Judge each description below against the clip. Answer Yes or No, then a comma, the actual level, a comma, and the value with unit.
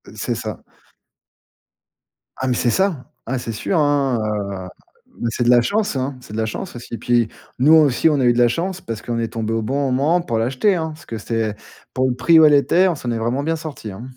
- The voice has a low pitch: Yes, low, 130 Hz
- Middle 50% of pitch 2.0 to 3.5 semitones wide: No, average, 5.1 semitones